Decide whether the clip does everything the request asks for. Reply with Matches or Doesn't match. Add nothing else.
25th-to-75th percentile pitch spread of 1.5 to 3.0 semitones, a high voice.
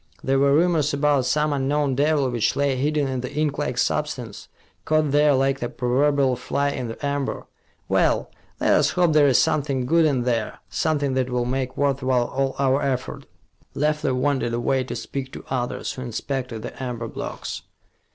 Doesn't match